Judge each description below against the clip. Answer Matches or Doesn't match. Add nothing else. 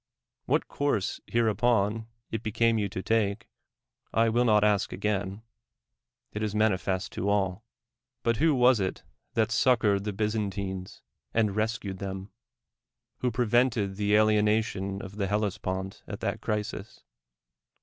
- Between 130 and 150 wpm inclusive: Matches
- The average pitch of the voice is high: Doesn't match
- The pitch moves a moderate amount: Doesn't match